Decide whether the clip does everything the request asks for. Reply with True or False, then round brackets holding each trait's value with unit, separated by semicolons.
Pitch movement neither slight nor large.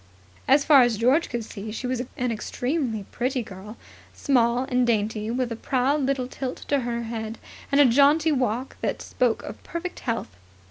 True (3.0 semitones)